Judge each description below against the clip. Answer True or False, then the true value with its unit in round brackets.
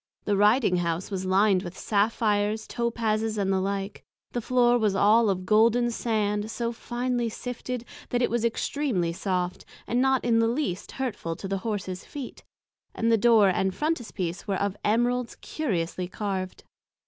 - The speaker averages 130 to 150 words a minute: False (160 wpm)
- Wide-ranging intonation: False (3.7 semitones)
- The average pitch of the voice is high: True (215 Hz)